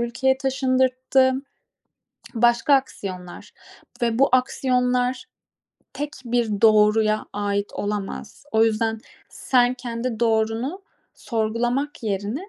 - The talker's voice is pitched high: Yes, high, 235 Hz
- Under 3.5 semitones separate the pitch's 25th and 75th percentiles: Yes, average, 2.9 semitones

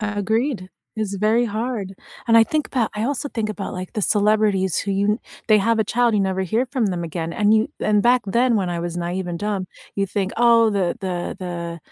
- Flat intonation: No, average, 3.1 semitones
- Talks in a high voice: Yes, high, 210 Hz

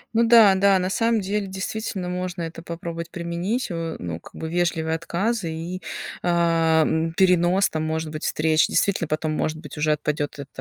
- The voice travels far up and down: No, average, 2.9 semitones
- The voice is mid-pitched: Yes, medium, 170 Hz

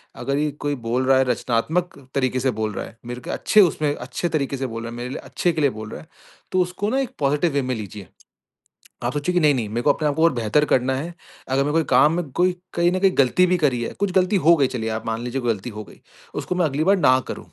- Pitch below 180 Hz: Yes, medium, 140 Hz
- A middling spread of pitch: No, wide, 5.7 semitones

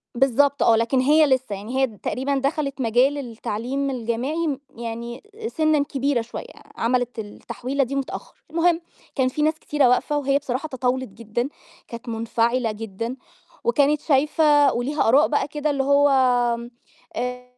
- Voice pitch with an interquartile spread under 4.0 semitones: Yes, average, 3.3 semitones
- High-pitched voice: Yes, very high, 265 Hz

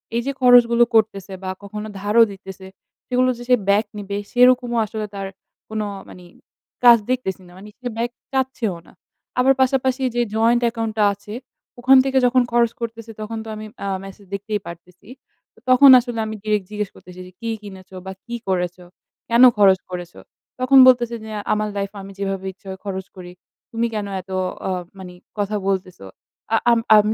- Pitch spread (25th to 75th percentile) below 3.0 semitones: No, average, 3.7 semitones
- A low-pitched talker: No, high, 215 Hz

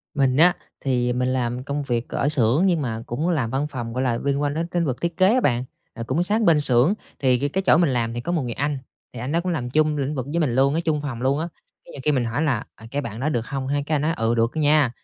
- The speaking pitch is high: No, medium, 140 Hz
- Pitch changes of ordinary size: Yes, average, 4.0 semitones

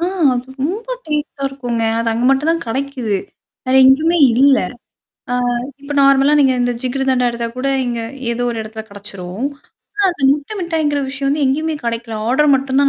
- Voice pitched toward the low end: No, very high, 270 Hz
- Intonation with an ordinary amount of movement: Yes, average, 3.3 semitones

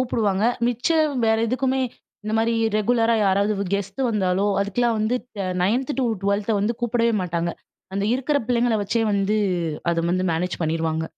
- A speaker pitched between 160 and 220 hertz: Yes, high, 215 Hz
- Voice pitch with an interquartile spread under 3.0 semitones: No, average, 4.0 semitones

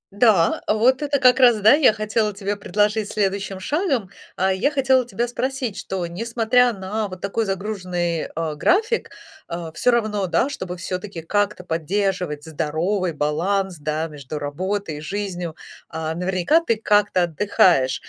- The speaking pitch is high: Yes, high, 195 Hz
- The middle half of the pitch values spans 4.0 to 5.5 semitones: Yes, average, 4.4 semitones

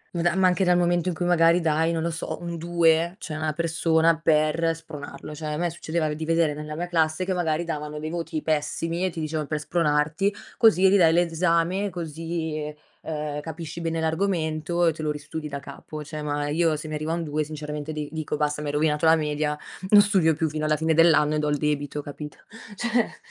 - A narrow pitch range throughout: Yes, narrow, 2.0 semitones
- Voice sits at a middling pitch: Yes, medium, 160 Hz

